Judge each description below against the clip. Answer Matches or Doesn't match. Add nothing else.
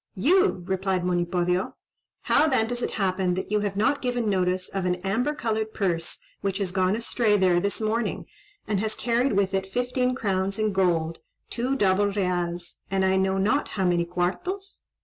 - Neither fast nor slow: Matches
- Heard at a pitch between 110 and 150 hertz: Doesn't match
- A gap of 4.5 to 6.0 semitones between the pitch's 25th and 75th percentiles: Doesn't match